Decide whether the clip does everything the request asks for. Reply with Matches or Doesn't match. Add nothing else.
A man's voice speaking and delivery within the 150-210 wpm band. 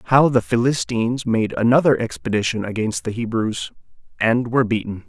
Doesn't match